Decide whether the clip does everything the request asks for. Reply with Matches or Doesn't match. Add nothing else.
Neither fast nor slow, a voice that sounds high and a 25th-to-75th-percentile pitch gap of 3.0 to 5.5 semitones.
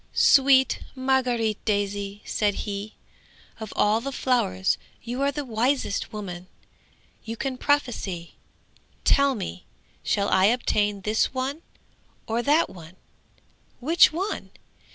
Doesn't match